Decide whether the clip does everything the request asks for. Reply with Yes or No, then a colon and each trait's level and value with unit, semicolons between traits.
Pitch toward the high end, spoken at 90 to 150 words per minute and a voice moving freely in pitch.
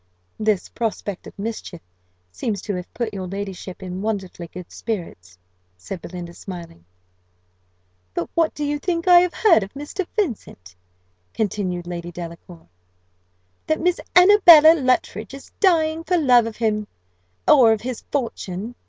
Yes: high, 215 Hz; average, 145 wpm; wide, 8.6 semitones